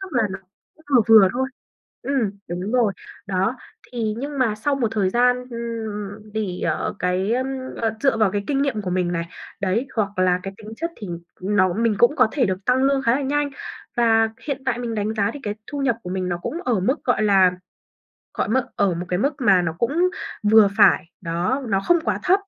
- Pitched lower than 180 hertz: No, high, 220 Hz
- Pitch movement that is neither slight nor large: Yes, average, 5.0 semitones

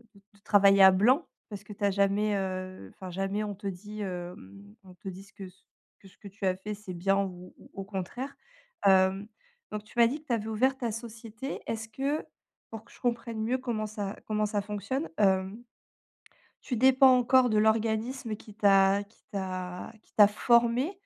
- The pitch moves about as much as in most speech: Yes, average, 3.1 semitones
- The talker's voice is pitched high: Yes, high, 210 Hz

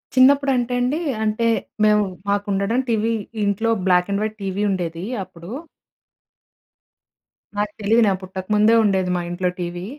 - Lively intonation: No, average, 3.3 semitones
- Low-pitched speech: No, high, 205 Hz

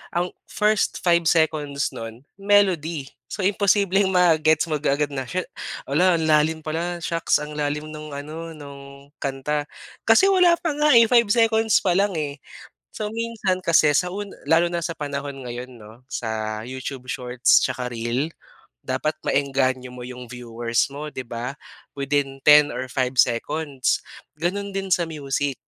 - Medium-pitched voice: Yes, medium, 150 Hz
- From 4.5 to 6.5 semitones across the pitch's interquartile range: Yes, average, 5.0 semitones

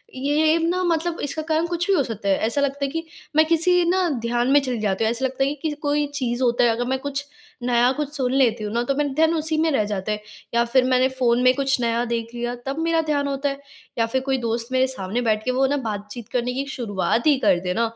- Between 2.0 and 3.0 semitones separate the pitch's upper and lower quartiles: No, average, 3.8 semitones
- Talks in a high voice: Yes, very high, 260 Hz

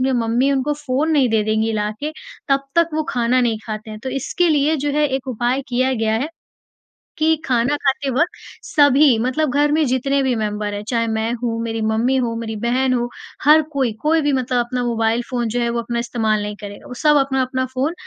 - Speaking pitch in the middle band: No, very high, 255 Hz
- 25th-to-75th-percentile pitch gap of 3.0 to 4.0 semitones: Yes, average, 3.4 semitones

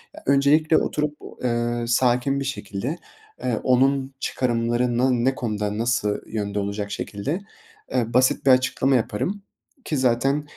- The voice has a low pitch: Yes, low, 125 Hz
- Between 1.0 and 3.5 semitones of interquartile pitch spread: Yes, average, 2.9 semitones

